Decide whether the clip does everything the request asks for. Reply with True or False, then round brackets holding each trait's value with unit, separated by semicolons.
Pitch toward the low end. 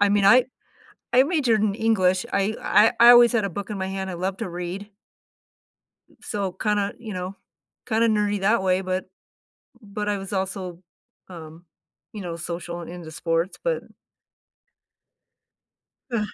False (195 Hz)